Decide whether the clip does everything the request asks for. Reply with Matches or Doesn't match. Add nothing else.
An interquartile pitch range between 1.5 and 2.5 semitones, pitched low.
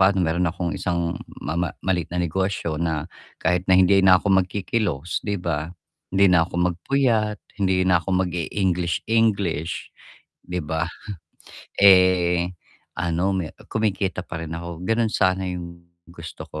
Matches